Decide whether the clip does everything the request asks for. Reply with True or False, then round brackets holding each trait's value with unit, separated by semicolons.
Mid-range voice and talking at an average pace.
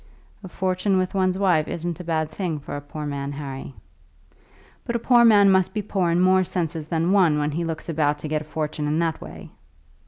False (165 Hz; 220 wpm)